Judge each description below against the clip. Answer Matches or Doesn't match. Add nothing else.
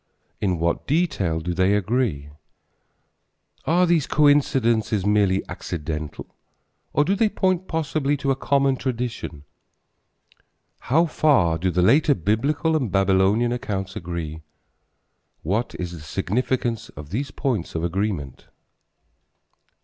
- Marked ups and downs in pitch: Matches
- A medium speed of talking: Doesn't match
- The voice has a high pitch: Doesn't match